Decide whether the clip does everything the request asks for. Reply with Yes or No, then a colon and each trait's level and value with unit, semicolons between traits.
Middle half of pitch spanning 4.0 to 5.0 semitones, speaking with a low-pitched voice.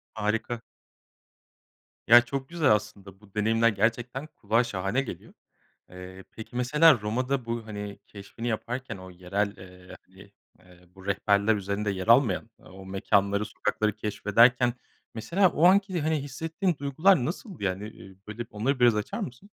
Yes: average, 4.4 semitones; low, 110 Hz